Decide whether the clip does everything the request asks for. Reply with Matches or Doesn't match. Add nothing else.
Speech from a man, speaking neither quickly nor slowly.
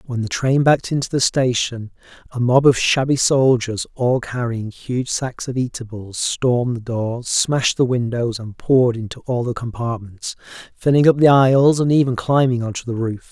Matches